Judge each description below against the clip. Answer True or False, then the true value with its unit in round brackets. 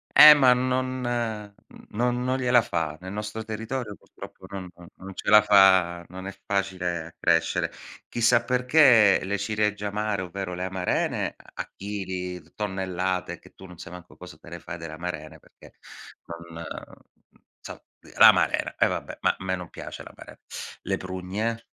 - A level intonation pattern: False (3.7 semitones)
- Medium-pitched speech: False (95 Hz)